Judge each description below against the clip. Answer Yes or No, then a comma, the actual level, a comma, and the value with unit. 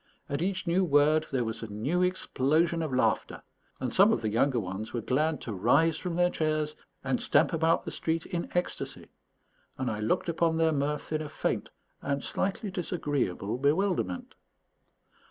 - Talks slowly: No, average, 175 wpm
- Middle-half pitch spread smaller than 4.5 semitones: No, average, 4.8 semitones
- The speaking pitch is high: No, medium, 155 Hz